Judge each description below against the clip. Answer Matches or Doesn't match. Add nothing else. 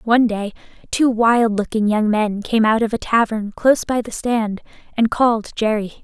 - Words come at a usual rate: Matches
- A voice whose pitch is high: Matches